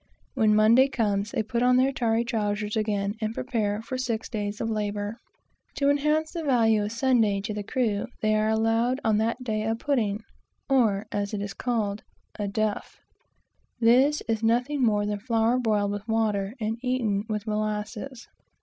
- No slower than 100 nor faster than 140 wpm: No, average, 175 wpm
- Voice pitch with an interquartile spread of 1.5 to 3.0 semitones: Yes, average, 2.7 semitones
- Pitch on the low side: No, high, 220 Hz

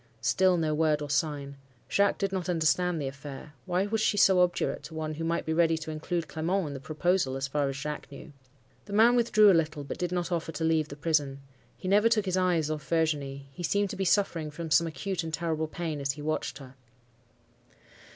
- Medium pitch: Yes, medium, 160 Hz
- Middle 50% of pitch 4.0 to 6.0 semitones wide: No, average, 3.3 semitones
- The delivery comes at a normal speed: No, fast, 225 wpm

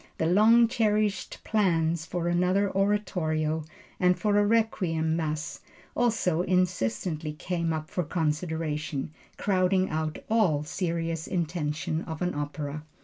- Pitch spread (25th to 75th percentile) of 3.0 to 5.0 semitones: Yes, average, 3.6 semitones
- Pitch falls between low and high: Yes, medium, 170 Hz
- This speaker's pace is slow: Yes, slow, 120 wpm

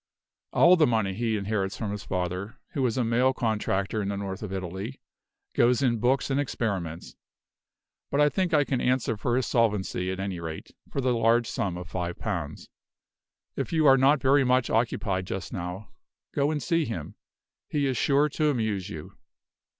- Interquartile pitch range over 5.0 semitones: Yes, wide, 5.4 semitones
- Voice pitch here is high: No, low, 115 Hz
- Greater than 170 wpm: Yes, average, 185 wpm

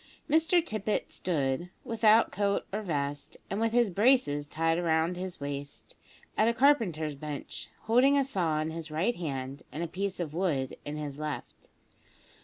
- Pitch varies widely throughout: Yes, wide, 6.5 semitones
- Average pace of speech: Yes, average, 165 wpm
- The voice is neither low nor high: Yes, medium, 170 Hz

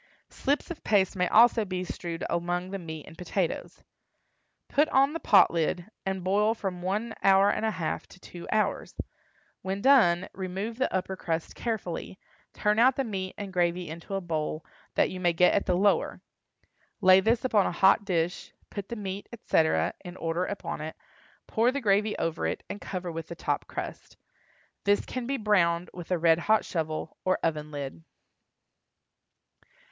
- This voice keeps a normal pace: Yes, average, 175 wpm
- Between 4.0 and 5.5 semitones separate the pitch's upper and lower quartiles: No, average, 3.5 semitones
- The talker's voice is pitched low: No, medium, 185 Hz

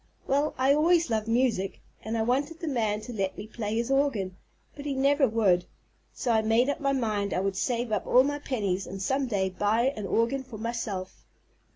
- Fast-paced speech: Yes, fast, 210 wpm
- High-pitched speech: Yes, high, 230 Hz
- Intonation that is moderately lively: Yes, average, 4.7 semitones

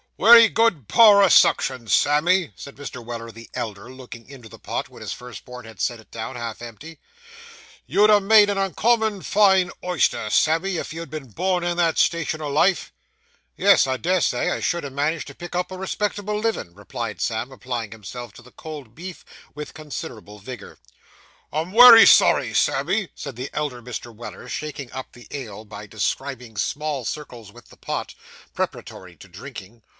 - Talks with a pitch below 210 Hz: Yes, medium, 140 Hz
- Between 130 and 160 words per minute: No, average, 180 wpm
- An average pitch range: No, wide, 7.3 semitones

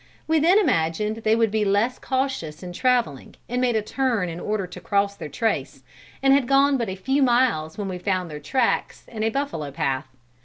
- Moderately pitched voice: No, high, 215 Hz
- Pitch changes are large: Yes, wide, 6.4 semitones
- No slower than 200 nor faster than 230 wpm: Yes, fast, 205 wpm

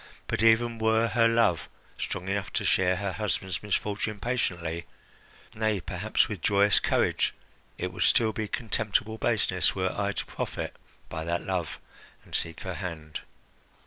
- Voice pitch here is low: Yes, low, 100 Hz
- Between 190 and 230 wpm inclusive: No, average, 150 wpm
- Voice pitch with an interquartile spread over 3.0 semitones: Yes, average, 3.4 semitones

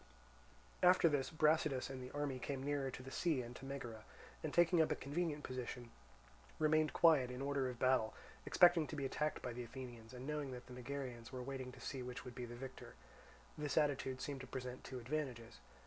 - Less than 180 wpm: No, fast, 205 wpm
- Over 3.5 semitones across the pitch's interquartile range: No, average, 2.8 semitones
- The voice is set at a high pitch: No, low, 130 Hz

